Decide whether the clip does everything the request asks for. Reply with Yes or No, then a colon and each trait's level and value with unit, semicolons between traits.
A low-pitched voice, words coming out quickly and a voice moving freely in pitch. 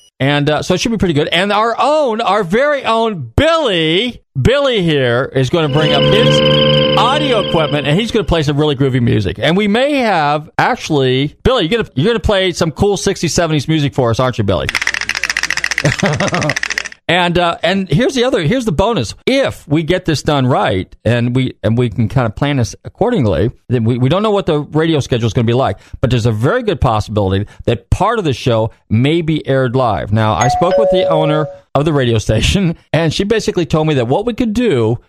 No: medium, 145 Hz; fast, 225 wpm; wide, 6.7 semitones